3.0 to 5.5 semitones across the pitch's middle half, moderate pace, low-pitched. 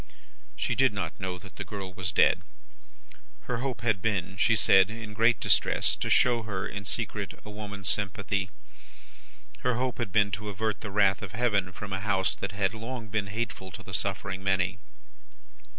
No: narrow, 2.5 semitones; average, 180 wpm; low, 100 Hz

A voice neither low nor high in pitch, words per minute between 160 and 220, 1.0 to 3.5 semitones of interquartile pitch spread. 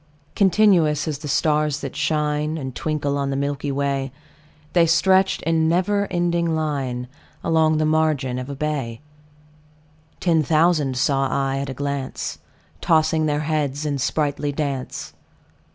No: medium, 150 Hz; average, 140 wpm; narrow, 2.5 semitones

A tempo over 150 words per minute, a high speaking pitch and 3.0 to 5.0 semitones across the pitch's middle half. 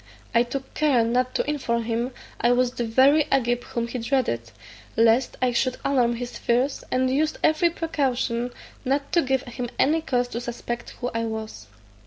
No: average, 180 wpm; high, 245 Hz; narrow, 2.4 semitones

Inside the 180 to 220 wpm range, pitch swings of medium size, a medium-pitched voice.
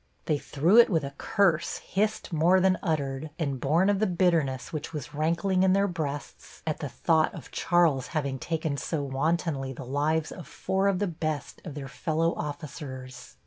Yes: average, 185 wpm; average, 3.9 semitones; medium, 155 Hz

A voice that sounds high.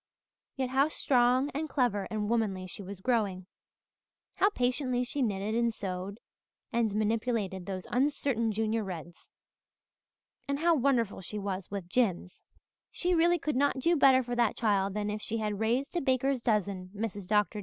Yes: high, 225 Hz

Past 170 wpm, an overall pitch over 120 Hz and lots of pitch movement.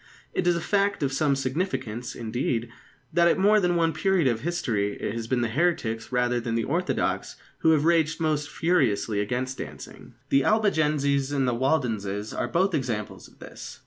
Yes: average, 180 wpm; low, 135 Hz; wide, 6.3 semitones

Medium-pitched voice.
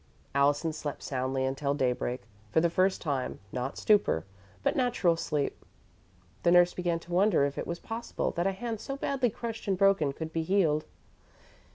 Yes: medium, 165 Hz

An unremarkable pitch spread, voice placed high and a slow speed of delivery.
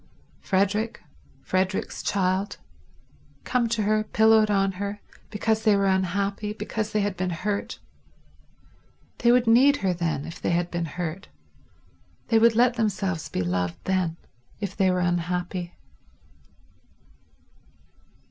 Yes: average, 3.4 semitones; high, 195 Hz; slow, 125 wpm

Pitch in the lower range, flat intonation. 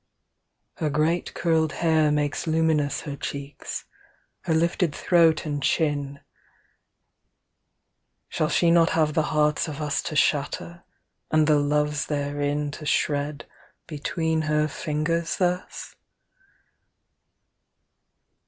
No: medium, 150 Hz; narrow, 1.8 semitones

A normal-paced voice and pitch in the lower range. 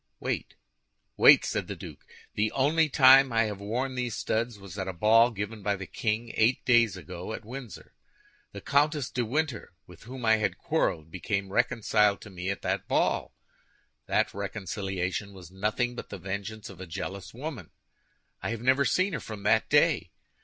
Yes: average, 180 wpm; low, 110 Hz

